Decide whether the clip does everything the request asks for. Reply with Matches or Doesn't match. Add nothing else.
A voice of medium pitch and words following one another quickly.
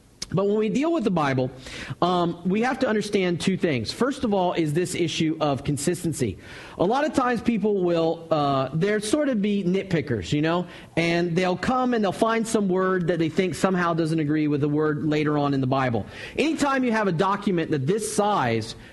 Matches